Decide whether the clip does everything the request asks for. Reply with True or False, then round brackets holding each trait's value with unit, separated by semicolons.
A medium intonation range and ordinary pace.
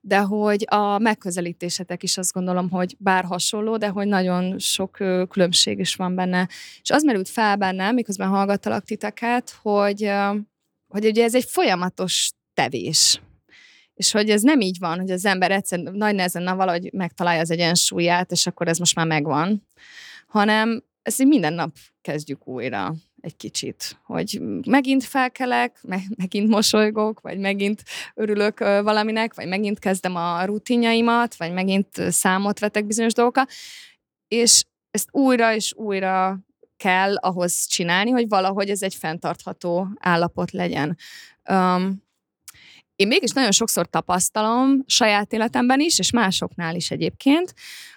True (3.5 semitones; 140 wpm)